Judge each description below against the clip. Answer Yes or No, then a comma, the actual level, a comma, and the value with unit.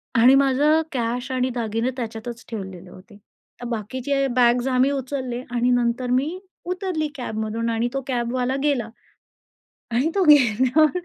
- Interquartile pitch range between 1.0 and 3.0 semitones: Yes, average, 2.7 semitones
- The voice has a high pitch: Yes, very high, 250 Hz